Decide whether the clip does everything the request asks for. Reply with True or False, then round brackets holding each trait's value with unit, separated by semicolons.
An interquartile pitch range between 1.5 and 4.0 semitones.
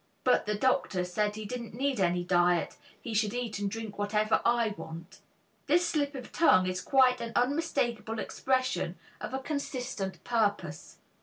False (4.7 semitones)